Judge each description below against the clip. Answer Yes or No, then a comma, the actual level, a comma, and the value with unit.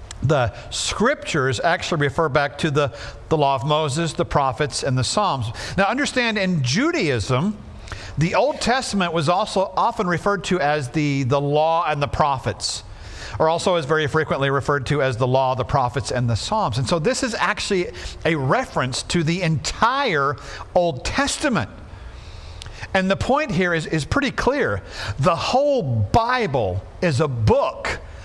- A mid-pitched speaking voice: Yes, medium, 145 Hz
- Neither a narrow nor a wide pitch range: No, wide, 7.2 semitones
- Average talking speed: Yes, average, 160 wpm